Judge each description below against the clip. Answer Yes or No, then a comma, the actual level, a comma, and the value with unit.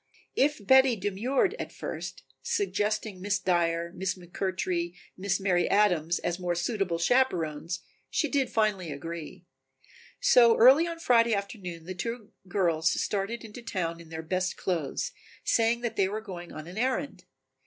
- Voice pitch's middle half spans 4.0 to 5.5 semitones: Yes, average, 5.1 semitones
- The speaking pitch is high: Yes, high, 195 Hz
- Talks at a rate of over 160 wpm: No, average, 155 wpm